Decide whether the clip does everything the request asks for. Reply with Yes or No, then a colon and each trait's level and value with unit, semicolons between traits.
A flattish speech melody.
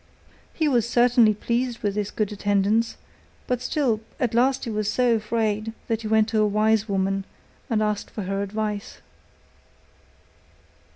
Yes: narrow, 2.2 semitones